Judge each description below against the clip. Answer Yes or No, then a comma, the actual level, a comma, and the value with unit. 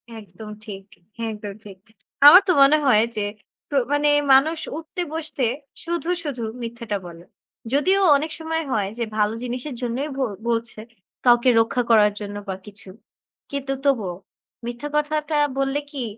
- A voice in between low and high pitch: No, very high, 250 Hz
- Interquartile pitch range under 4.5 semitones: No, wide, 5.4 semitones